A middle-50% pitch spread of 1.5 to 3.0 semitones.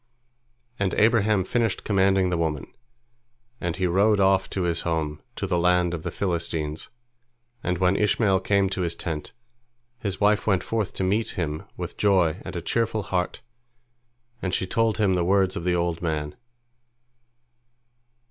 Yes: average, 2.7 semitones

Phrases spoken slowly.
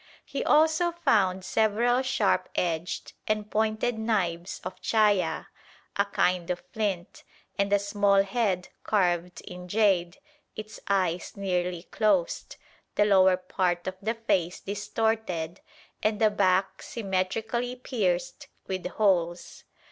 Yes: slow, 120 wpm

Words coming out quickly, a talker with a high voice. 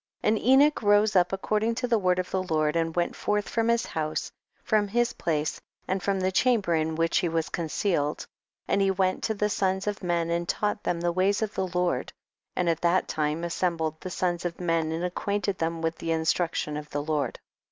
No: fast, 220 wpm; medium, 180 Hz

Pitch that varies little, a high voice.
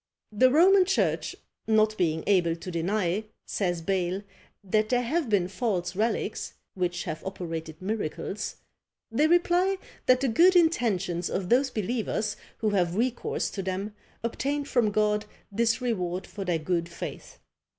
No: wide, 5.5 semitones; high, 210 Hz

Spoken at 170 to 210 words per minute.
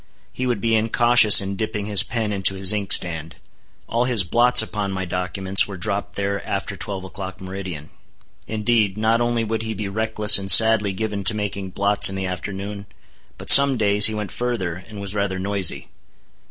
Yes: average, 180 wpm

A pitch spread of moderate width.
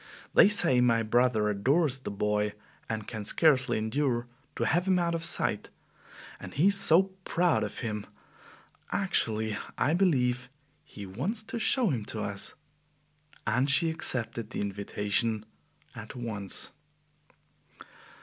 No: wide, 7.3 semitones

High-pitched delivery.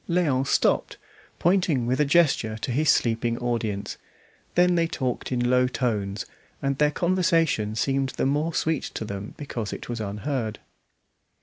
No: low, 130 Hz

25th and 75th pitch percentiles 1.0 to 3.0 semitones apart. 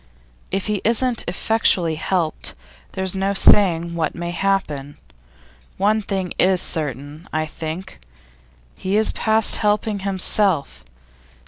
No: average, 4.0 semitones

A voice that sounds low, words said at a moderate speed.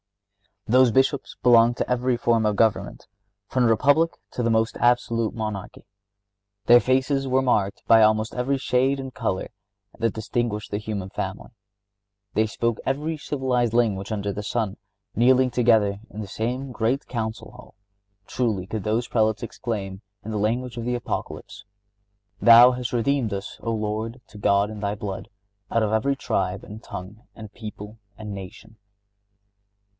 Yes: low, 115 Hz; average, 160 wpm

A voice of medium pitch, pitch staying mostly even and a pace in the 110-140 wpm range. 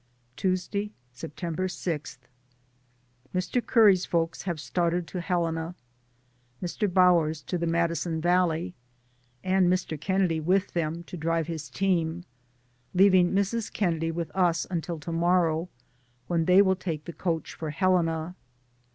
Yes: medium, 175 Hz; narrow, 2.1 semitones; slow, 135 wpm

